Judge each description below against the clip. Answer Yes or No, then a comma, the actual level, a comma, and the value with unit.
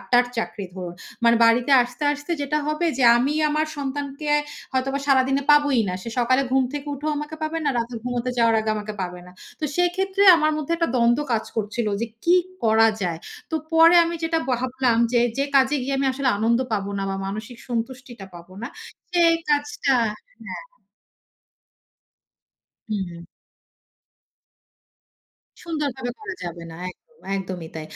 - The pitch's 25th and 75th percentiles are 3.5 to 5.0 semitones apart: Yes, average, 4.7 semitones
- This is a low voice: No, very high, 255 Hz